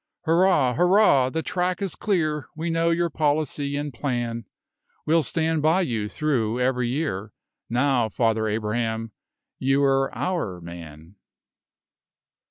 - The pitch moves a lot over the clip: Yes, wide, 6.0 semitones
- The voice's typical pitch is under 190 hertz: Yes, low, 135 Hz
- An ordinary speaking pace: No, slow, 120 wpm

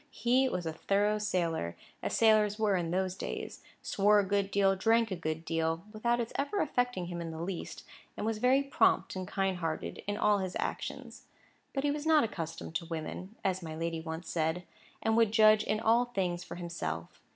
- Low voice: No, high, 195 Hz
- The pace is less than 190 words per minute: No, average, 195 wpm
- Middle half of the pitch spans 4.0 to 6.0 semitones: Yes, average, 4.8 semitones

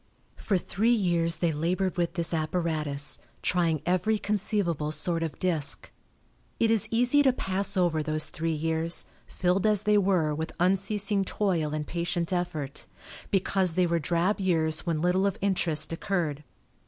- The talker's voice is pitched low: No, medium, 175 Hz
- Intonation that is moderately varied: Yes, average, 3.3 semitones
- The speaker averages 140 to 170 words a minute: Yes, average, 155 wpm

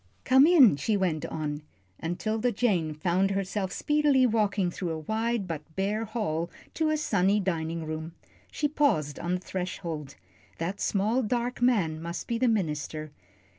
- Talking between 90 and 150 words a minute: No, average, 160 wpm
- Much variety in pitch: Yes, wide, 6.0 semitones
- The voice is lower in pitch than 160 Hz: No, high, 195 Hz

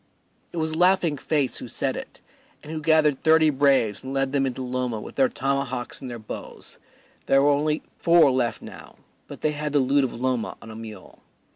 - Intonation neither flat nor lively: Yes, average, 3.3 semitones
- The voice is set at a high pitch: No, medium, 140 Hz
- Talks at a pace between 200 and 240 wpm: Yes, fast, 205 wpm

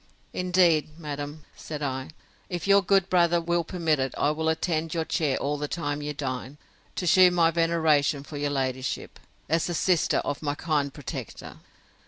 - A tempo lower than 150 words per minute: No, average, 175 wpm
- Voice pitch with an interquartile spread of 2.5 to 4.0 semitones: Yes, average, 2.9 semitones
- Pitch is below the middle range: No, medium, 155 Hz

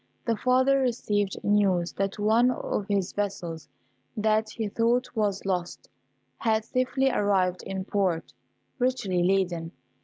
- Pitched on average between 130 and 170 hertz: No, high, 205 Hz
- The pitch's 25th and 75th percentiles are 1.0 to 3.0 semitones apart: No, average, 3.5 semitones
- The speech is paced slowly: Yes, slow, 125 wpm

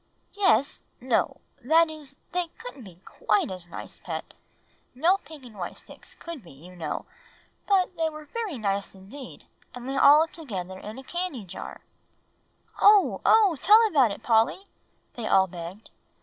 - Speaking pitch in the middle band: No, very high, 270 Hz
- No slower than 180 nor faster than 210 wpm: No, average, 165 wpm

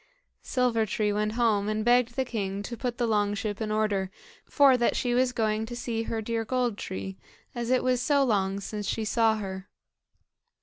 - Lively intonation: No, average, 2.8 semitones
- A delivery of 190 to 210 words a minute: Yes, average, 200 wpm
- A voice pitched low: No, high, 225 Hz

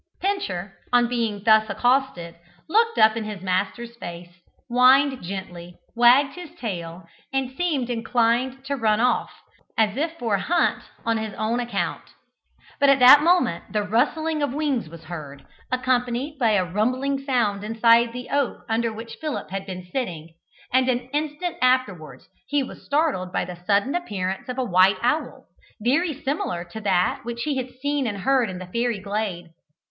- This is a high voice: Yes, high, 235 Hz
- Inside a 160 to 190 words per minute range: Yes, average, 170 wpm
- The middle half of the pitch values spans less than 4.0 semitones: No, average, 5.3 semitones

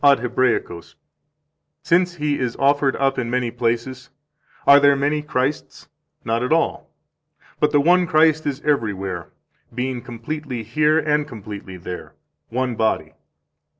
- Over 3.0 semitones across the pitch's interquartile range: Yes, average, 4.2 semitones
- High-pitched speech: No, low, 130 Hz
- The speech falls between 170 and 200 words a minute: No, average, 140 wpm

